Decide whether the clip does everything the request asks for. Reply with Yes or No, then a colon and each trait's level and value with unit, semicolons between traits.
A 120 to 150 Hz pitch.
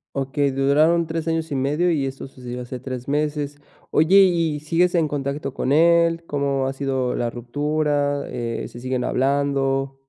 Yes: medium, 140 Hz